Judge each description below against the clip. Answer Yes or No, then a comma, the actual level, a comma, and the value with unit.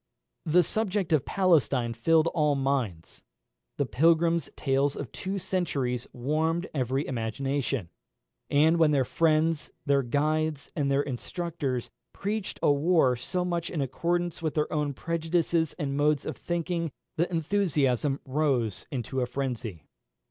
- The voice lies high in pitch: No, medium, 150 Hz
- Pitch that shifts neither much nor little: Yes, average, 3.9 semitones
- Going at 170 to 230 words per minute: No, slow, 135 wpm